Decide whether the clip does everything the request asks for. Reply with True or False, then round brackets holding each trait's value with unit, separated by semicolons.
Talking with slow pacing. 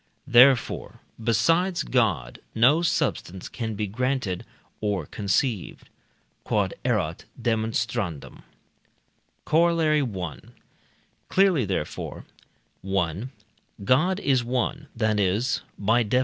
True (85 wpm)